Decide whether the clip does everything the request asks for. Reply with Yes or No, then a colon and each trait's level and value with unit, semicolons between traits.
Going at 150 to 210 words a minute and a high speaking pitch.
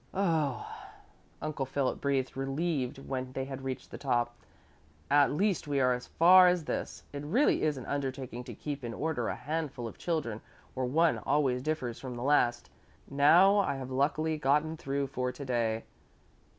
No: average, 170 wpm; medium, 140 Hz